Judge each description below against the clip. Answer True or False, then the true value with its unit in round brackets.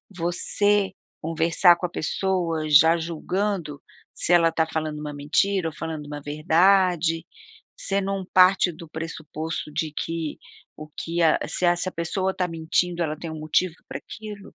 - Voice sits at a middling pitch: True (165 Hz)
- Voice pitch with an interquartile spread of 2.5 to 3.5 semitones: True (2.8 semitones)